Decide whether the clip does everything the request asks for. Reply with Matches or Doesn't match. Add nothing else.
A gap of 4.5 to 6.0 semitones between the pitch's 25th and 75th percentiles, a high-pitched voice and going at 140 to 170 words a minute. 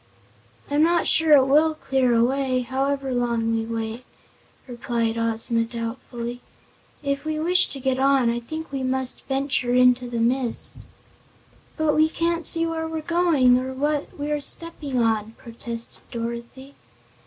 Doesn't match